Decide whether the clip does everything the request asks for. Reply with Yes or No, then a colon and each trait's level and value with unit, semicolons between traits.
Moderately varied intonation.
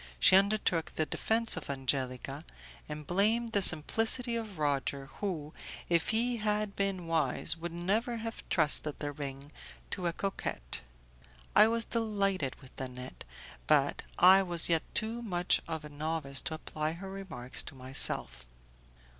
No: wide, 6.2 semitones